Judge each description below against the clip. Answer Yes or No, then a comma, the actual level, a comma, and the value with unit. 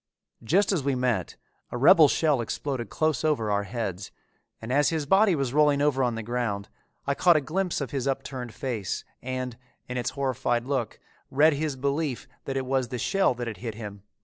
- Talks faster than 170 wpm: Yes, average, 200 wpm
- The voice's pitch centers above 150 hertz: No, low, 130 Hz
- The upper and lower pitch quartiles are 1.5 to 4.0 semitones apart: Yes, average, 3.6 semitones